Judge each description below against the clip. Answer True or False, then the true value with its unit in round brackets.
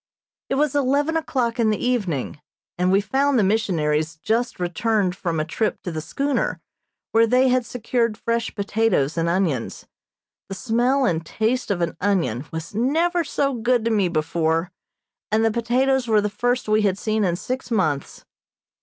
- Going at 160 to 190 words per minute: True (170 wpm)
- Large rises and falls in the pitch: True (6.0 semitones)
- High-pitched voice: True (220 Hz)